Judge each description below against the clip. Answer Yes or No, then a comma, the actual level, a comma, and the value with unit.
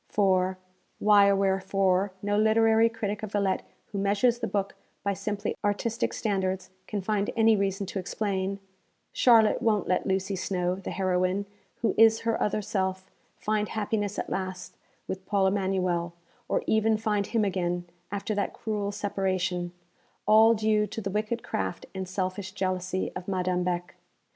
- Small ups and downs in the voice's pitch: Yes, narrow, 2.2 semitones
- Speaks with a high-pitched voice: Yes, high, 200 Hz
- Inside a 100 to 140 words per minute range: No, average, 160 wpm